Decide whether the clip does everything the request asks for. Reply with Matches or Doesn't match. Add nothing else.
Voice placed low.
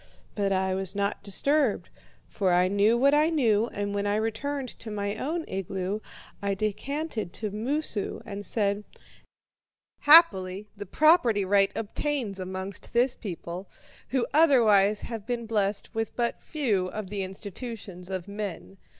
Doesn't match